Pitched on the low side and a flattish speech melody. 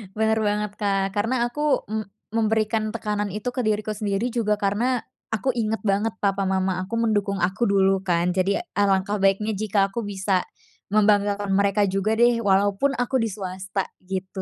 No: high, 205 Hz; narrow, 2.1 semitones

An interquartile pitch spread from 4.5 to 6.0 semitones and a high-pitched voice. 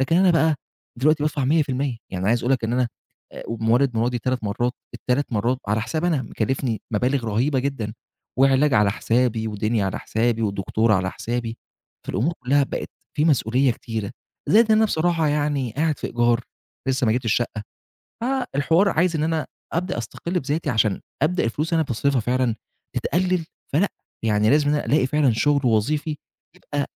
No: average, 5.0 semitones; low, 130 Hz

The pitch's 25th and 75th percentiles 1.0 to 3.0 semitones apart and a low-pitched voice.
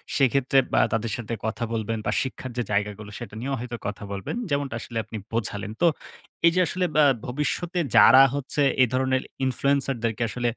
No: average, 3.4 semitones; low, 125 Hz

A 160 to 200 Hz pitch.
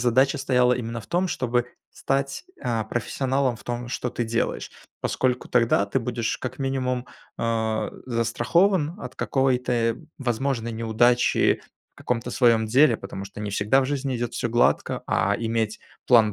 No: low, 120 Hz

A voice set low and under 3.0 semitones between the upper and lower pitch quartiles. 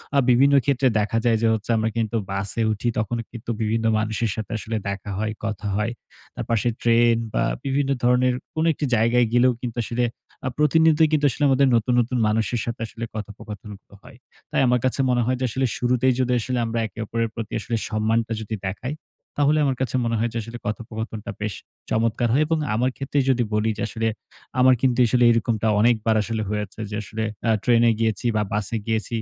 Yes: low, 115 Hz; narrow, 2.4 semitones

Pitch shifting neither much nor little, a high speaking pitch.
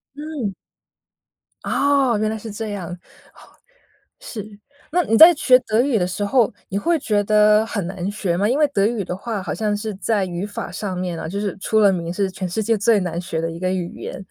Yes: average, 3.4 semitones; high, 205 Hz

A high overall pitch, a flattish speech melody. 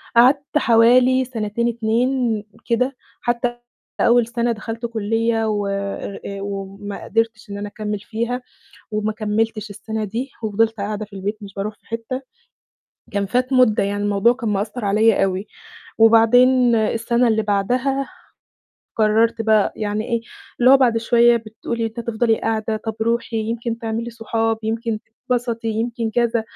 Yes: high, 225 Hz; narrow, 1.8 semitones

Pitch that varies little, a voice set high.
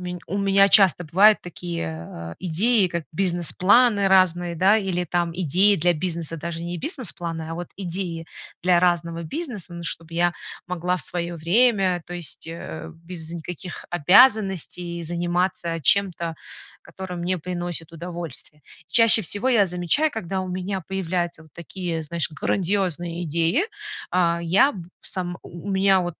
No: narrow, 2.3 semitones; medium, 175 Hz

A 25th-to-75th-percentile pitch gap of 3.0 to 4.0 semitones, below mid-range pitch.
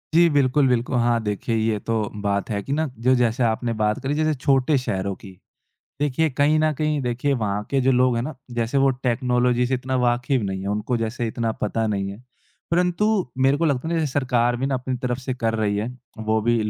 Yes: average, 3.5 semitones; low, 125 Hz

